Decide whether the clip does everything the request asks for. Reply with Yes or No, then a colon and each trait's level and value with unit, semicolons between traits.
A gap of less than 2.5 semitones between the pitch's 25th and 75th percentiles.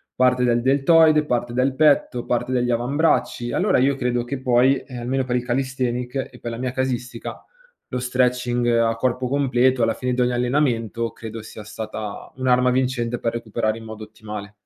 Yes: narrow, 1.6 semitones